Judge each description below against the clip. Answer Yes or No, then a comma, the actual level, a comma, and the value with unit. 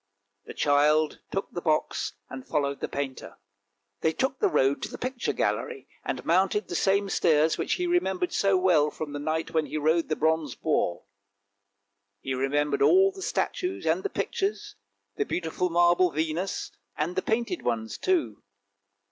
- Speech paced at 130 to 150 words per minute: No, average, 165 wpm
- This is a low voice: No, medium, 165 Hz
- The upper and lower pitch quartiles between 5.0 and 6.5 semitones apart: Yes, wide, 5.4 semitones